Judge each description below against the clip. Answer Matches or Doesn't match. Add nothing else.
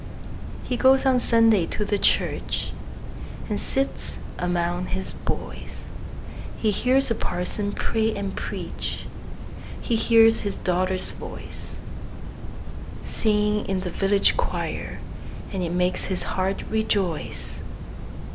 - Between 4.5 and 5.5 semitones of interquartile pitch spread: Doesn't match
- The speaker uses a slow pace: Matches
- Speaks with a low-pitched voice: Doesn't match